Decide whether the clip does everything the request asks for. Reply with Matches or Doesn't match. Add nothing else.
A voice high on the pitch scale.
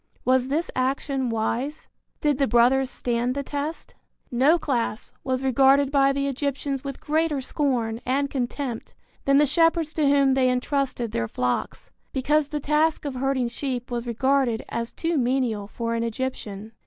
Matches